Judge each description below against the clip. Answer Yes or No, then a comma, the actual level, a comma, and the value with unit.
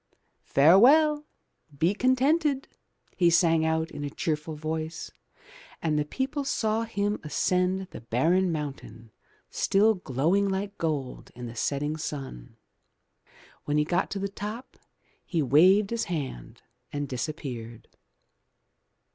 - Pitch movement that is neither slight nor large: No, wide, 5.7 semitones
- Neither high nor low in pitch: Yes, medium, 165 Hz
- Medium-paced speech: No, slow, 120 wpm